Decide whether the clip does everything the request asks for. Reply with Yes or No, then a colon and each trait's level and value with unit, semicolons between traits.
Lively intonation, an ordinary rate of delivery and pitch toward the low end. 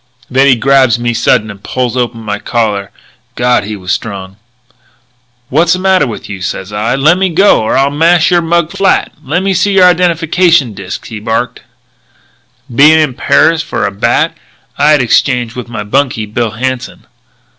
Yes: wide, 6.6 semitones; average, 170 wpm; low, 130 Hz